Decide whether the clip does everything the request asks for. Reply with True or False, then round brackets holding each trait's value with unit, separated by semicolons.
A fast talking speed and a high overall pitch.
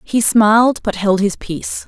False (190 wpm; 210 Hz)